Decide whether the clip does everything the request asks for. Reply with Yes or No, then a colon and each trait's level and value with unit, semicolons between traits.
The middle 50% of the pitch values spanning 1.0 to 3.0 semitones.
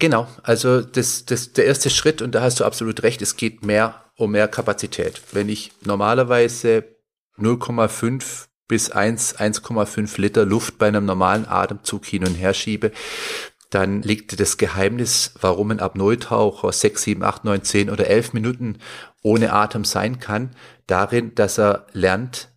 Yes: average, 2.7 semitones